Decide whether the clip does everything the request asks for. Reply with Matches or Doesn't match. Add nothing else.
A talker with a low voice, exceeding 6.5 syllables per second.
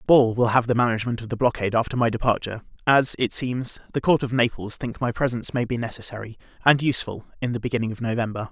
Matches